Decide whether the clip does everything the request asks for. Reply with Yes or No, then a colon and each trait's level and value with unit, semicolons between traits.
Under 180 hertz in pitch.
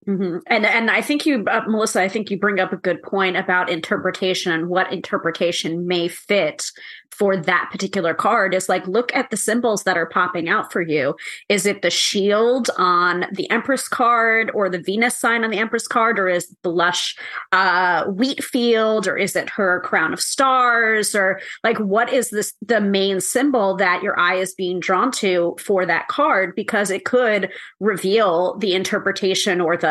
No: high, 195 Hz